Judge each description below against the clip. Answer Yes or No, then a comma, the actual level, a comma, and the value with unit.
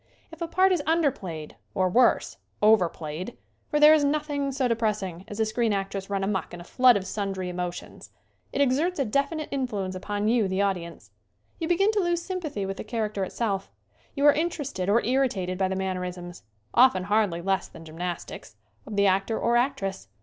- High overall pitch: Yes, high, 210 Hz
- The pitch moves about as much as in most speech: No, wide, 6.7 semitones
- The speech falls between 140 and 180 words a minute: No, average, 195 wpm